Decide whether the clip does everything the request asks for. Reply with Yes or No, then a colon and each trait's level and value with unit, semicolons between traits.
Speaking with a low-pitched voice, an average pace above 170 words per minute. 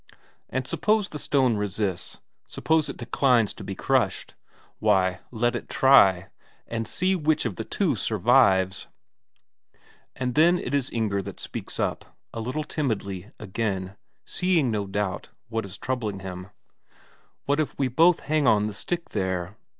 No: low, 115 Hz; average, 150 wpm